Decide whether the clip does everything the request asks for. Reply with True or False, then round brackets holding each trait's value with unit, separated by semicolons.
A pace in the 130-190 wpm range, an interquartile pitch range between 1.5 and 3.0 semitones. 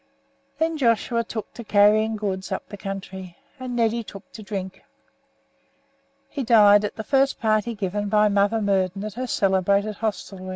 True (160 wpm; 2.4 semitones)